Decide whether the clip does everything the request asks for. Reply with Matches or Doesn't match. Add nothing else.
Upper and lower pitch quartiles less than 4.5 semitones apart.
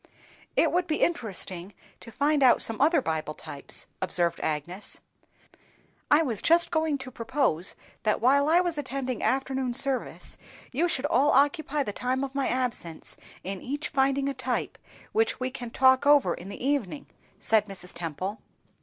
Doesn't match